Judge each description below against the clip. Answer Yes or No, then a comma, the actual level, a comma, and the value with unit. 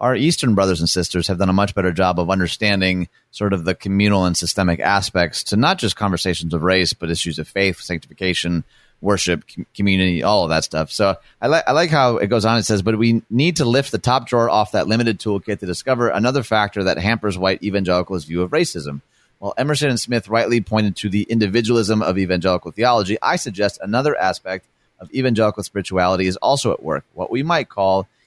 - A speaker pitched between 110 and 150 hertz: No, low, 100 Hz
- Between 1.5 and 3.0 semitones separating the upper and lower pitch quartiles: No, average, 3.7 semitones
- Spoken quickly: Yes, fast, 210 wpm